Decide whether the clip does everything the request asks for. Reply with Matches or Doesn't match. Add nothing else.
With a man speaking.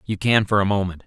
Matches